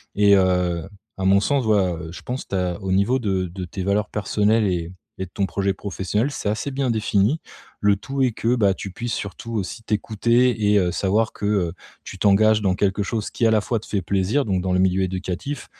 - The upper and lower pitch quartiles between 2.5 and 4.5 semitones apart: Yes, average, 3.0 semitones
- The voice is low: Yes, low, 100 Hz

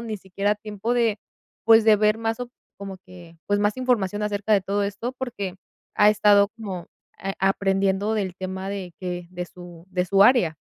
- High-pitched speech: Yes, high, 200 Hz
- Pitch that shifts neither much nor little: No, narrow, 2.3 semitones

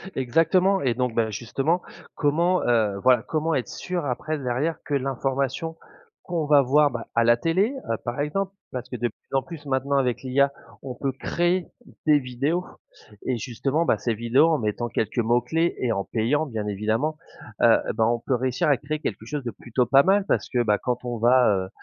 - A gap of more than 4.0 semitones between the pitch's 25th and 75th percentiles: Yes, average, 4.5 semitones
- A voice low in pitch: Yes, low, 130 Hz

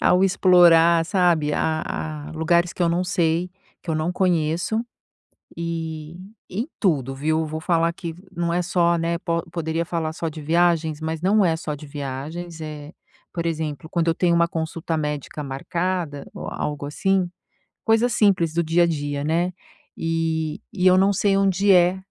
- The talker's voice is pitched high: No, medium, 165 Hz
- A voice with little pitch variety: Yes, narrow, 2.1 semitones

